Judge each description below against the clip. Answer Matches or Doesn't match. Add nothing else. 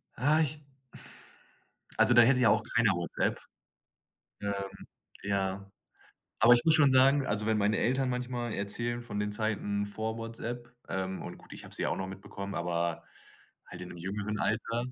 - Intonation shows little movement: Doesn't match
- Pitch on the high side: Doesn't match